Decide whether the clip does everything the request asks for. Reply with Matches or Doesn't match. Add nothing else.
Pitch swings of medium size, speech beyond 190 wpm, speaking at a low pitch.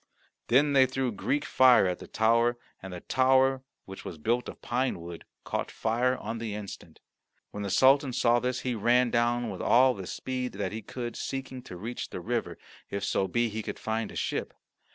Matches